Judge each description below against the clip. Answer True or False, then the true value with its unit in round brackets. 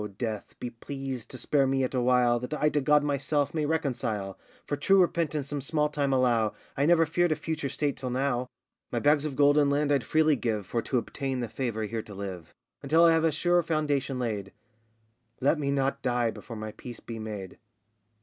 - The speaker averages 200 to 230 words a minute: True (205 wpm)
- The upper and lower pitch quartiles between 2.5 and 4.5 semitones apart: True (3.8 semitones)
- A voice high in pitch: False (135 Hz)